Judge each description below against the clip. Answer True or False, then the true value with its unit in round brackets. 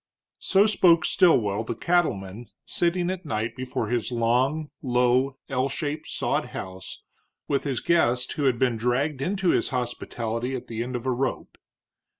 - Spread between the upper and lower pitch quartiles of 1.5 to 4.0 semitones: False (4.6 semitones)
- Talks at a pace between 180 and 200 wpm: False (155 wpm)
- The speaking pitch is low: True (130 Hz)